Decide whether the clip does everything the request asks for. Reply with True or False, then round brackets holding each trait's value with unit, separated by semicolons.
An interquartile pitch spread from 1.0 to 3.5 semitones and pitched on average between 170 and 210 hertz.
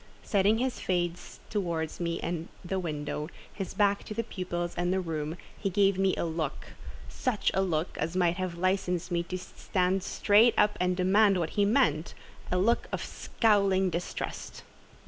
True (2.7 semitones; 185 Hz)